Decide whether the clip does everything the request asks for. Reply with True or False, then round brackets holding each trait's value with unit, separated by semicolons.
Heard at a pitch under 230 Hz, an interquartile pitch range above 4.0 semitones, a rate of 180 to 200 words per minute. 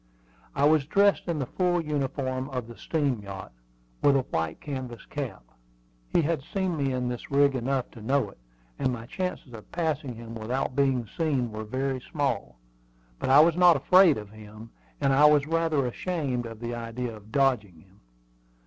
True (135 Hz; 4.4 semitones; 185 wpm)